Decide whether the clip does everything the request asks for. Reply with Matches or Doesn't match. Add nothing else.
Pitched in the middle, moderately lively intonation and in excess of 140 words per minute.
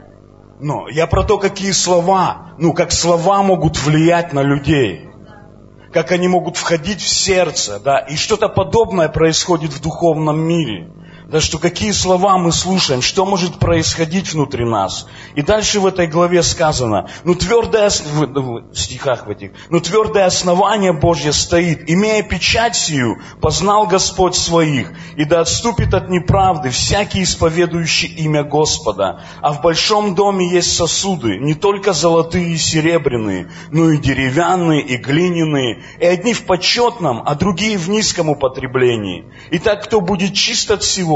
Matches